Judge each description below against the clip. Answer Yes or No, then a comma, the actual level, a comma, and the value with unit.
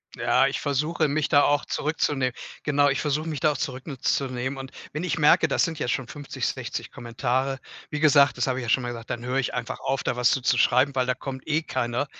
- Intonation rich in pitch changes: No, narrow, 2.6 semitones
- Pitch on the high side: No, low, 135 Hz